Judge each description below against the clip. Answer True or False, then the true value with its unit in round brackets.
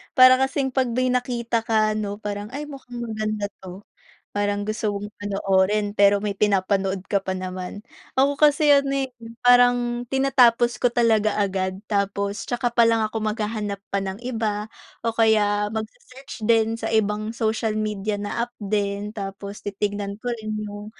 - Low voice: False (215 Hz)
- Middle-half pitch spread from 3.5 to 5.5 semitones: False (2.8 semitones)